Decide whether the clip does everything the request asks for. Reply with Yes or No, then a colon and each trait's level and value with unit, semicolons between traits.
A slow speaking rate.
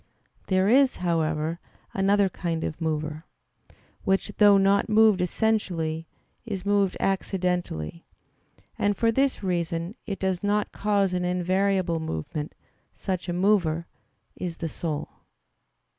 Yes: slow, 120 wpm